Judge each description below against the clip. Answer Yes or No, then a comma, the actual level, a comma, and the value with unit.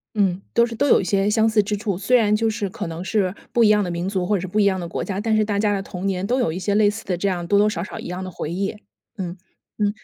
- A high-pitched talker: Yes, high, 200 Hz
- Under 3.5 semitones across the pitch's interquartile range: Yes, narrow, 2.5 semitones